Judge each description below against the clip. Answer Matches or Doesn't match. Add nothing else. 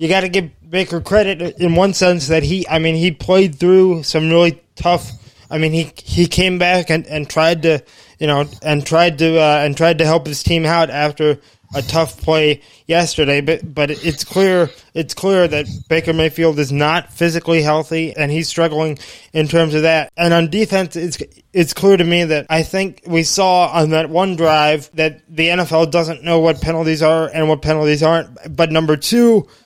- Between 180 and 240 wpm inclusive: Matches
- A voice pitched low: Doesn't match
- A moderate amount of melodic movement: Doesn't match